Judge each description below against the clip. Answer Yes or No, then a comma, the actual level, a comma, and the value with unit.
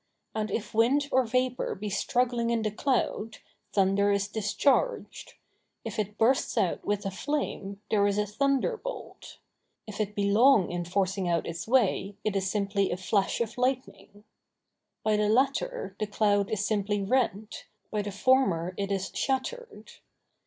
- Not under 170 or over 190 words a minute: No, average, 160 wpm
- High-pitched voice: Yes, high, 210 Hz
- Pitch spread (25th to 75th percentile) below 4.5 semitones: Yes, average, 4.0 semitones